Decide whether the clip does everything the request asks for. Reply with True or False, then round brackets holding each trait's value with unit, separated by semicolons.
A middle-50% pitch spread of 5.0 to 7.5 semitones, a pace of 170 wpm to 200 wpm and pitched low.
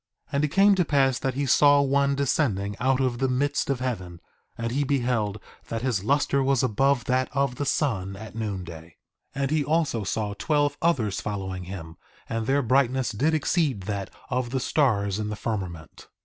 True (5.3 semitones; 195 wpm; 125 Hz)